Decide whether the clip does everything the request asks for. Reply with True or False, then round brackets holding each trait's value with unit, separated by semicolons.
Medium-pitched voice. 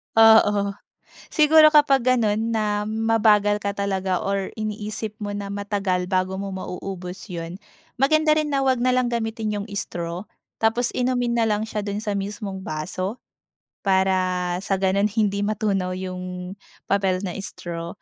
False (205 Hz)